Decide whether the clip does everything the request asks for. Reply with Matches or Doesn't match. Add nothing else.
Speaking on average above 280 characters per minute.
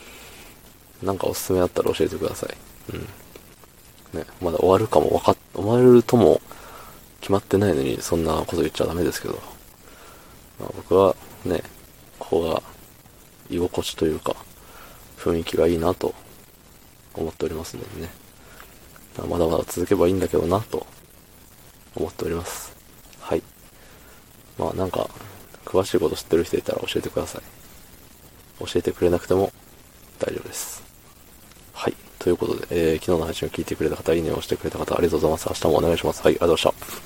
Matches